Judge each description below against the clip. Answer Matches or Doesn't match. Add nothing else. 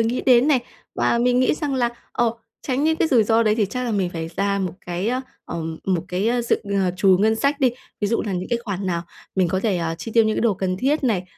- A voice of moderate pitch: Doesn't match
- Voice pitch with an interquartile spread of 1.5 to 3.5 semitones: Doesn't match